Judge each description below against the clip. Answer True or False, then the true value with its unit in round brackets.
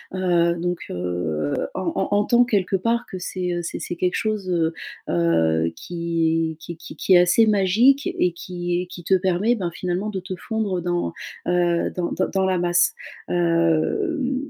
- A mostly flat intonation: True (2.2 semitones)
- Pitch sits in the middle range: True (180 Hz)